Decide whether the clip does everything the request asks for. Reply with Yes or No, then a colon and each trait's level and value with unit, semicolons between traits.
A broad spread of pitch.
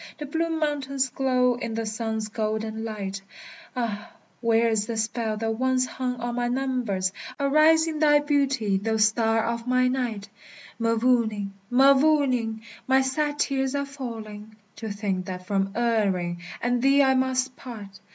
No: average, 3.5 semitones